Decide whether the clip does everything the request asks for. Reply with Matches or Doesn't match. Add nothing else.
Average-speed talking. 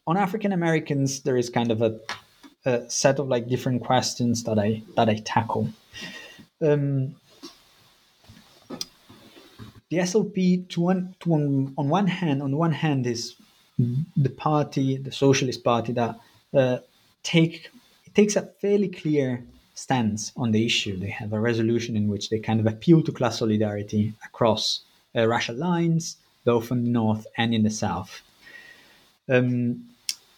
Matches